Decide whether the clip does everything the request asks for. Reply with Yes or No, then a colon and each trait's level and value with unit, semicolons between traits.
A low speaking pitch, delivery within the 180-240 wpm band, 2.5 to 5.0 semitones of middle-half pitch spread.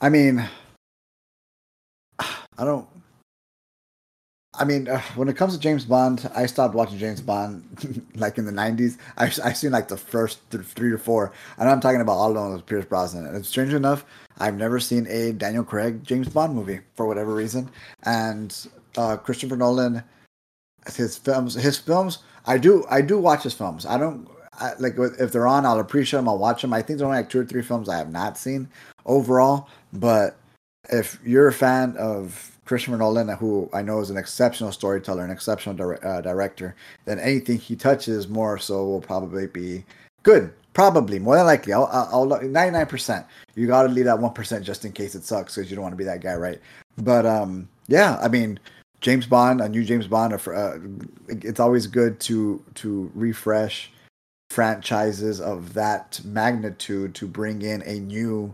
Yes: low, 115 Hz; average, 190 wpm; average, 3.5 semitones